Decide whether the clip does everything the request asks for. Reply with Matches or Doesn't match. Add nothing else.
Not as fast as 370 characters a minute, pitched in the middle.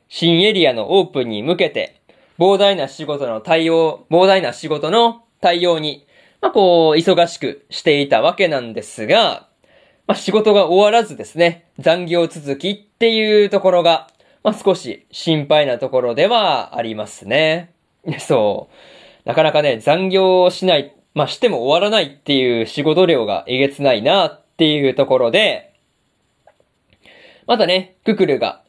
Matches